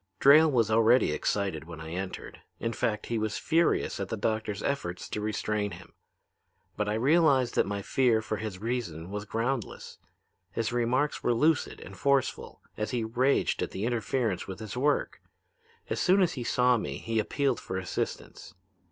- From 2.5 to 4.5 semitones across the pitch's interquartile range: Yes, average, 3.8 semitones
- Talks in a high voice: No, low, 110 Hz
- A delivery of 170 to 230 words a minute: Yes, average, 175 wpm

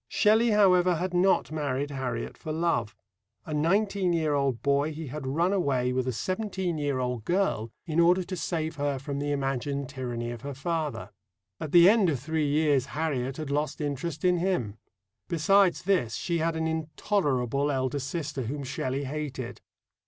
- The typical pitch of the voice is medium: Yes, medium, 150 Hz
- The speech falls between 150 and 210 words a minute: Yes, average, 175 wpm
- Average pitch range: Yes, average, 4.3 semitones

